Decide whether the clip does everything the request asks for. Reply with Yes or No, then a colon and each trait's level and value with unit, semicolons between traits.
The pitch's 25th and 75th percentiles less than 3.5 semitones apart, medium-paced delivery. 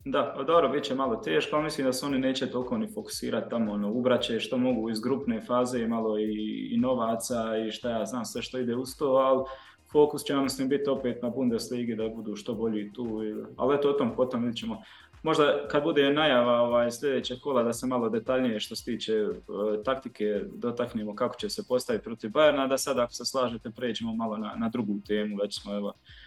No: average, 3.0 semitones; fast, 215 wpm